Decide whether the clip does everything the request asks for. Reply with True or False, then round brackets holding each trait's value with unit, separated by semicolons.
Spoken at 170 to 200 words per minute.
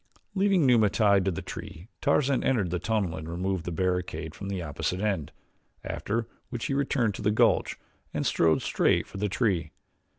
True (185 wpm)